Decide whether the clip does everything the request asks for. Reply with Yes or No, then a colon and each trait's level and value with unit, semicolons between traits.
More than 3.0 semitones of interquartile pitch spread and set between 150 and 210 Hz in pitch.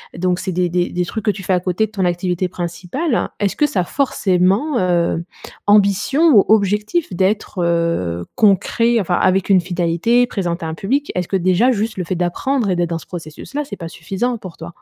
Yes: average, 3.6 semitones; medium, 185 Hz